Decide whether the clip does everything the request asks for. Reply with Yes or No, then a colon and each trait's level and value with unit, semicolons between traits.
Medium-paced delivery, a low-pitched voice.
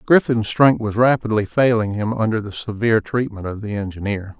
Yes: average, 180 wpm; low, 110 Hz